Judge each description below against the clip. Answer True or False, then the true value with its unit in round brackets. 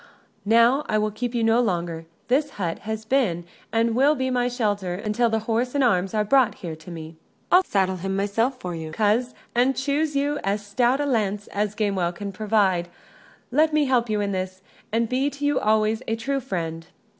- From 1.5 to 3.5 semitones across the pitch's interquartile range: False (4.6 semitones)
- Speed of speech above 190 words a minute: True (200 wpm)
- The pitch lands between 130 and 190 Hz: False (220 Hz)